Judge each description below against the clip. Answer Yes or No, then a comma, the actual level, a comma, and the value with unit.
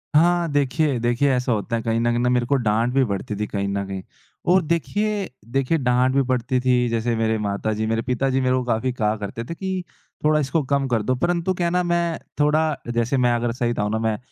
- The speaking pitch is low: Yes, low, 125 Hz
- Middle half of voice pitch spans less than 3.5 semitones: No, average, 4.7 semitones